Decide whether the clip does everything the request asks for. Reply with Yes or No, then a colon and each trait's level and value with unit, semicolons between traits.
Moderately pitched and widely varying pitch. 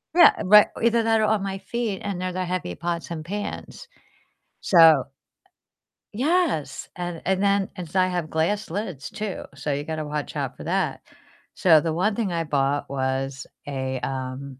Yes: medium, 175 Hz; wide, 5.7 semitones